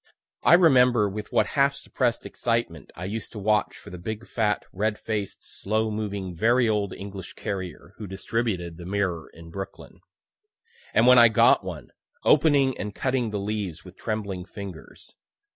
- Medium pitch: No, low, 105 Hz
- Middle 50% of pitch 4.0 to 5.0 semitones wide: No, average, 3.4 semitones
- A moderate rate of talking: Yes, average, 160 wpm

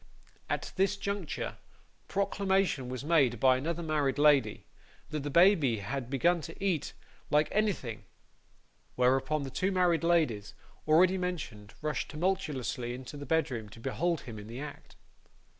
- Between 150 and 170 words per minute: No, average, 140 wpm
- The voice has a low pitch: No, medium, 150 Hz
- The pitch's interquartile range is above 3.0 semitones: Yes, wide, 5.4 semitones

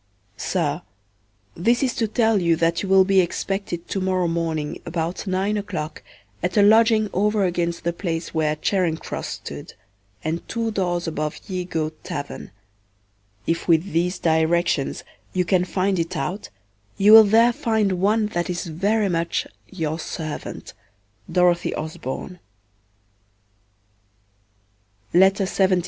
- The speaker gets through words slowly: Yes, slow, 130 wpm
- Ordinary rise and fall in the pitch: Yes, average, 3.5 semitones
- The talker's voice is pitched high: No, medium, 180 Hz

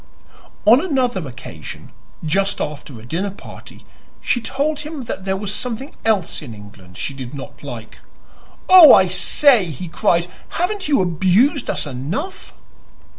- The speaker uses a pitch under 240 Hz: Yes, high, 190 Hz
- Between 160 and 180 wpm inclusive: No, average, 145 wpm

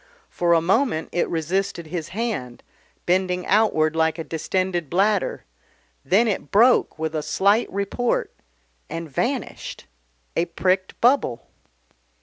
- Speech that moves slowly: Yes, slow, 125 wpm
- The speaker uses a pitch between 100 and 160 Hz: No, medium, 180 Hz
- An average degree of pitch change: Yes, average, 4.1 semitones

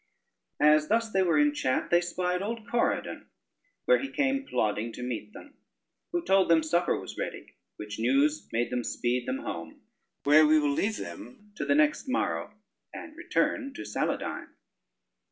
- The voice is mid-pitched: Yes, medium, 170 Hz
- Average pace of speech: Yes, average, 170 wpm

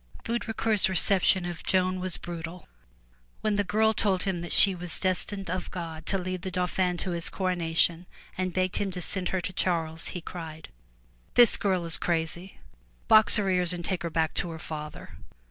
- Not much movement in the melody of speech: Yes, narrow, 2.0 semitones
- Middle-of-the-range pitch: Yes, medium, 180 Hz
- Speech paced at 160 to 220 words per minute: Yes, average, 185 wpm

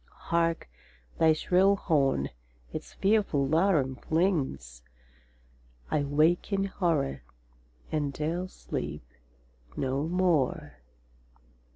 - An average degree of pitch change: Yes, average, 4.8 semitones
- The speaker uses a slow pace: Yes, slow, 85 wpm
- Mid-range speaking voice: Yes, medium, 155 Hz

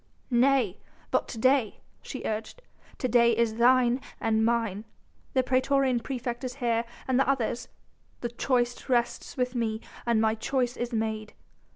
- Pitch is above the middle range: Yes, high, 240 Hz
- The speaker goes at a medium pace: Yes, average, 155 wpm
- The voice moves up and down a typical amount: No, narrow, 2.2 semitones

